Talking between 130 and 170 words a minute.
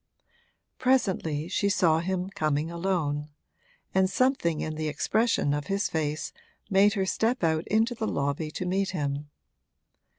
Yes: average, 140 wpm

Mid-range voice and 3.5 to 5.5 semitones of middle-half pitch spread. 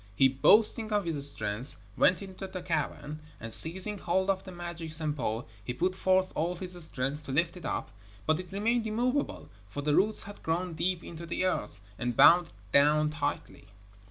Yes: medium, 170 Hz; average, 4.2 semitones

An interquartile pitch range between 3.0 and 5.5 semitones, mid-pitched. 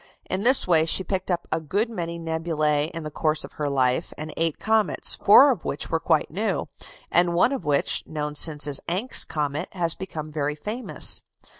Yes: average, 3.5 semitones; medium, 160 Hz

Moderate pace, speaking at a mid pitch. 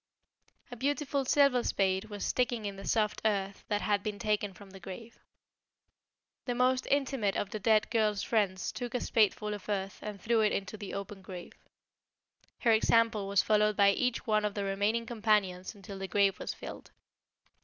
No: average, 180 wpm; high, 210 Hz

